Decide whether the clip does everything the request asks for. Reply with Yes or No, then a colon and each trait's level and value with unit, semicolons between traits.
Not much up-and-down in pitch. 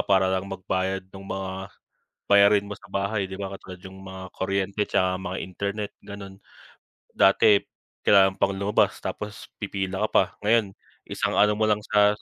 Yes: narrow, 1.3 semitones